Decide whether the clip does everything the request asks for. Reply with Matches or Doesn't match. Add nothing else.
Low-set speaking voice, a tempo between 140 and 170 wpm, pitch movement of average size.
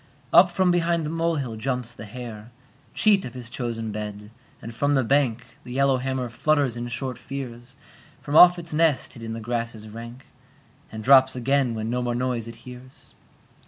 Doesn't match